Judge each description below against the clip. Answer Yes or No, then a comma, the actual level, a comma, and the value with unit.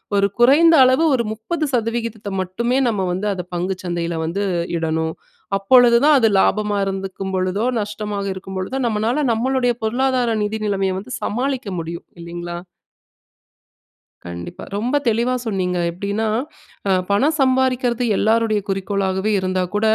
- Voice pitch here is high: Yes, high, 210 Hz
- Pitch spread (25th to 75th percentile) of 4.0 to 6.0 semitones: Yes, average, 4.4 semitones